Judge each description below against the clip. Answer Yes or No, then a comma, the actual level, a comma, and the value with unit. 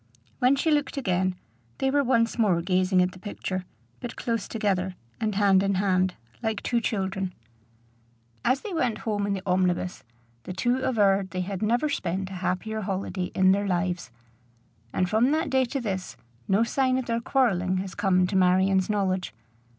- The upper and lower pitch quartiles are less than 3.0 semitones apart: No, average, 3.9 semitones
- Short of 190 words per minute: Yes, average, 175 wpm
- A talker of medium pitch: No, high, 195 Hz